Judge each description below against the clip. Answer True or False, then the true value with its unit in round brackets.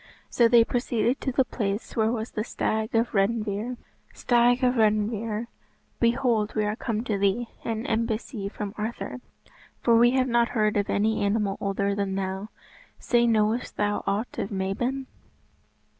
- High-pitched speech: True (220 Hz)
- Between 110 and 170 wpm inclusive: True (160 wpm)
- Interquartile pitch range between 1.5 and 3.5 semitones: True (2.5 semitones)